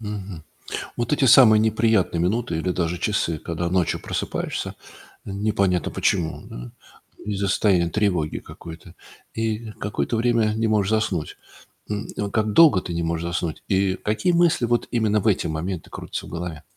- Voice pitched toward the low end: Yes, low, 100 Hz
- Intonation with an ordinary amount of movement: Yes, average, 4.1 semitones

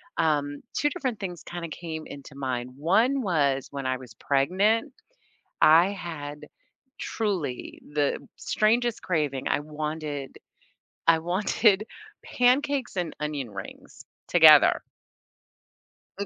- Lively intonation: Yes, wide, 6.1 semitones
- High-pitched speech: No, medium, 160 Hz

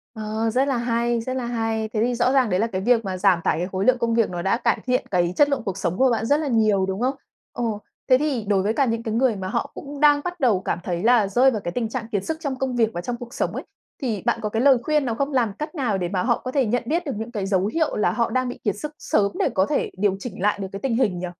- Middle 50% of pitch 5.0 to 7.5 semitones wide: No, average, 4.3 semitones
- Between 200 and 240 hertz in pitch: Yes, high, 230 Hz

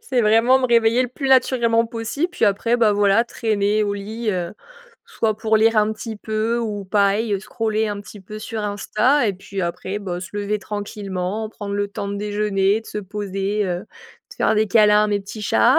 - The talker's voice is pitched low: No, high, 210 Hz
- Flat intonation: Yes, narrow, 1.9 semitones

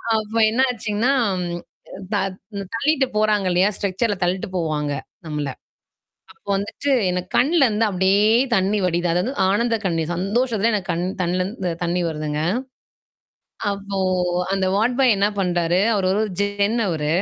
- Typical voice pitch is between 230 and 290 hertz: No, high, 200 Hz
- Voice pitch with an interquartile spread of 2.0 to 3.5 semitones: No, average, 3.9 semitones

